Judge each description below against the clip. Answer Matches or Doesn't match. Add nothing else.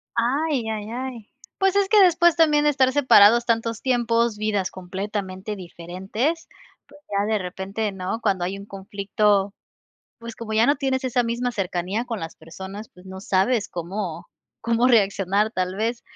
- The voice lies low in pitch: Doesn't match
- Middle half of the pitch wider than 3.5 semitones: Matches